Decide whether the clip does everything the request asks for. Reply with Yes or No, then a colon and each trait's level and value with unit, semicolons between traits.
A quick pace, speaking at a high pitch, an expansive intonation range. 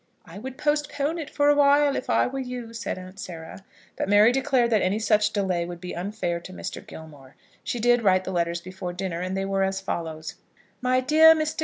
Yes: fast, 210 wpm; high, 205 Hz; wide, 6.3 semitones